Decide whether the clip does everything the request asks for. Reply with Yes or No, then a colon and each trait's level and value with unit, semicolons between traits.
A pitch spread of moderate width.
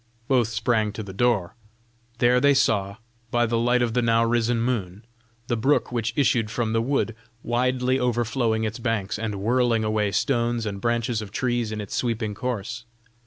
No: narrow, 2.0 semitones